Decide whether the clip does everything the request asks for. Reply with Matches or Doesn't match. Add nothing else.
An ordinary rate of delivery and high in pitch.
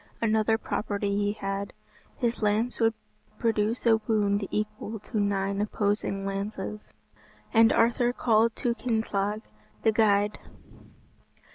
Doesn't match